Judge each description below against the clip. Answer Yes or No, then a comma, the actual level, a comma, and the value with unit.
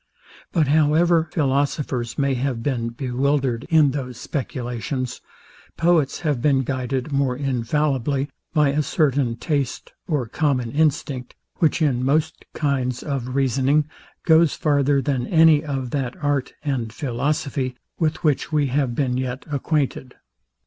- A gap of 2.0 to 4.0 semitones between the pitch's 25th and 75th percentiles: Yes, average, 2.9 semitones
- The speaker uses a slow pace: Yes, slow, 130 wpm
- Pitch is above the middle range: No, medium, 140 Hz